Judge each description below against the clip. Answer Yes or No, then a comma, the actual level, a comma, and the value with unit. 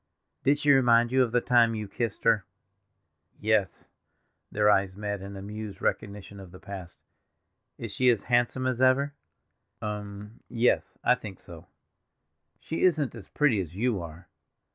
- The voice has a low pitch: Yes, low, 110 Hz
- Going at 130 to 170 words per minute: Yes, average, 145 wpm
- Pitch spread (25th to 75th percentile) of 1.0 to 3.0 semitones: No, average, 3.9 semitones